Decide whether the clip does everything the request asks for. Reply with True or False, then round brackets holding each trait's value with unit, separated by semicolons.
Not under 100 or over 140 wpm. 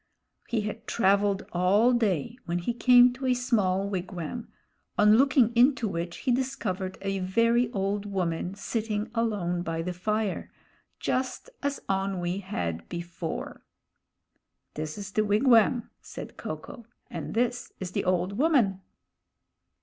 True (135 wpm)